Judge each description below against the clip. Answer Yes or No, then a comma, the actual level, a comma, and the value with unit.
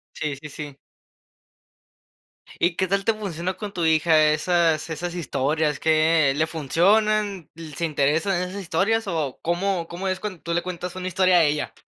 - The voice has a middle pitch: Yes, medium, 170 Hz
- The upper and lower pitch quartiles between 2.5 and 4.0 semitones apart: Yes, average, 3.2 semitones